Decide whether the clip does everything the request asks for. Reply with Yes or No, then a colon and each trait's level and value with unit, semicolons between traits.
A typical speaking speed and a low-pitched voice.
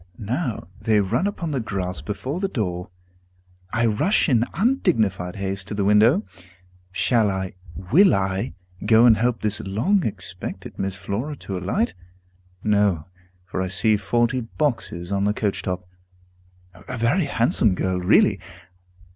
Yes: average, 145 wpm; low, 105 Hz